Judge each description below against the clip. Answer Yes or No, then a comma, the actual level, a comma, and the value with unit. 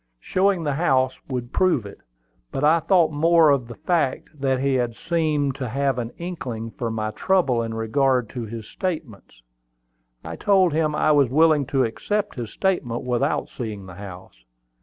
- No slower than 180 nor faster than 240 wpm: No, average, 170 wpm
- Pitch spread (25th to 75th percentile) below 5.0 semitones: No, wide, 5.5 semitones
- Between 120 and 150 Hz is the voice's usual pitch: Yes, low, 135 Hz